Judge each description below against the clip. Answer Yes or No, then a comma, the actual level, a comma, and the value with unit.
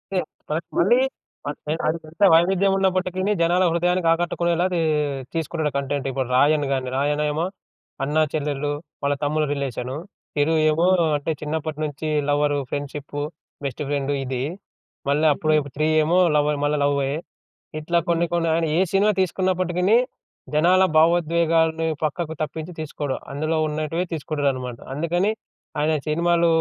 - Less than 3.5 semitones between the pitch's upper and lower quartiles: Yes, average, 2.9 semitones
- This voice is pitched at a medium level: Yes, medium, 155 Hz